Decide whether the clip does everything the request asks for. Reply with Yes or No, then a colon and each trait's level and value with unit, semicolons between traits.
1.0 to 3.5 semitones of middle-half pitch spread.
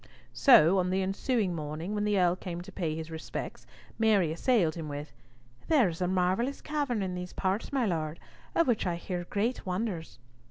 No: average, 4.3 semitones